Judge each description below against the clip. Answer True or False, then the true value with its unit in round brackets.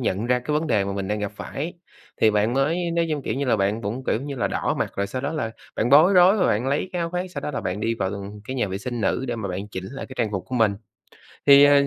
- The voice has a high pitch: False (125 Hz)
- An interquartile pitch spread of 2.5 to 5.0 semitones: False (5.6 semitones)